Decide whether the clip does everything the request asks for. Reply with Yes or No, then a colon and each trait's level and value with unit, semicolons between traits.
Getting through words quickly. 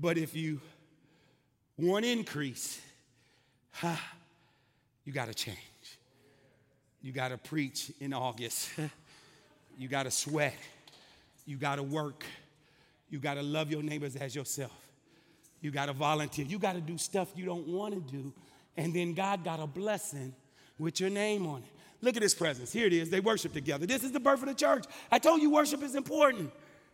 No: average, 180 wpm